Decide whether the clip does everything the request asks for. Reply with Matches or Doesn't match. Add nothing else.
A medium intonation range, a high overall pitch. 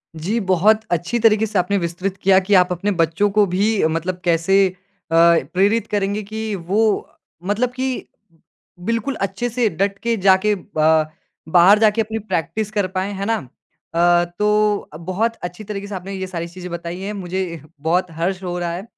Matches